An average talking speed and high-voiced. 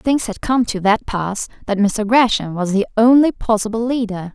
Yes: average, 195 wpm; high, 220 Hz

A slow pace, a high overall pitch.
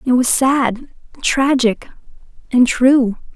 Yes: slow, 90 wpm; very high, 255 Hz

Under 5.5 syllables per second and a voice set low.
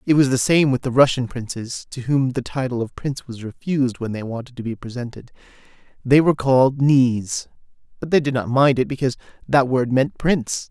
No: 5.7 syllables/s; low, 130 Hz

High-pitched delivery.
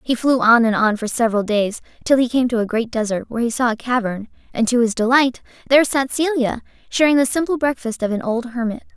Yes: high, 240 Hz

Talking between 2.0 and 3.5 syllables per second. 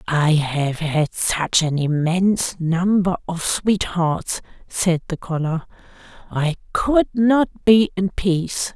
Yes: 3.4 syllables/s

